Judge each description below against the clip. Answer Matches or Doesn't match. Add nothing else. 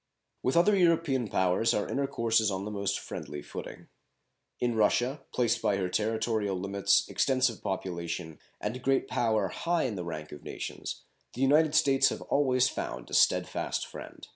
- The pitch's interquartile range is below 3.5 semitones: Doesn't match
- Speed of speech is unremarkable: Matches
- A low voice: Matches